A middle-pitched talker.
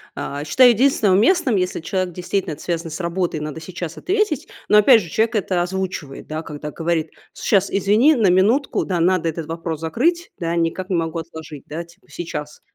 Yes: medium, 175 Hz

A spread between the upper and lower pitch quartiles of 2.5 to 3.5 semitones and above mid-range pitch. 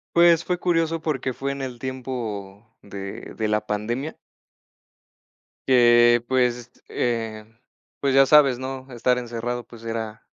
No: average, 2.8 semitones; low, 120 Hz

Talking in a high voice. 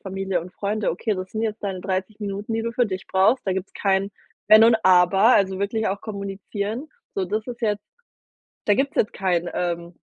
Yes: high, 200 Hz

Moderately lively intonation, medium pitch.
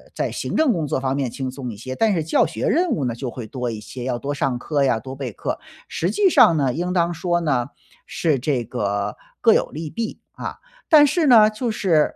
No: wide, 6.2 semitones; medium, 145 Hz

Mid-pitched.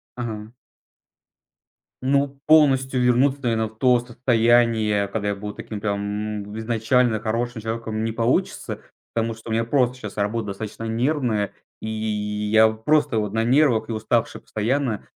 No: low, 115 Hz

